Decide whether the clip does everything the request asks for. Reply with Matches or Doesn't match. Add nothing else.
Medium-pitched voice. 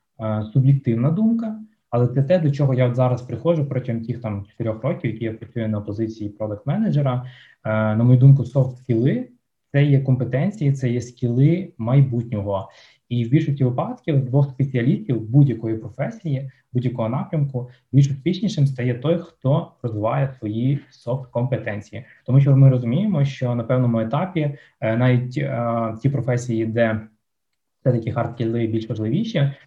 Doesn't match